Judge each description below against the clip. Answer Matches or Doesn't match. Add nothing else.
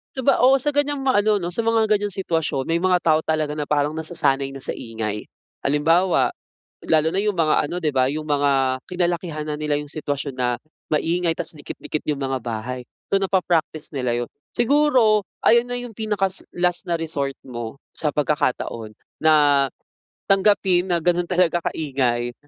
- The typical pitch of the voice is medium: Matches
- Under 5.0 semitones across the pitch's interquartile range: Doesn't match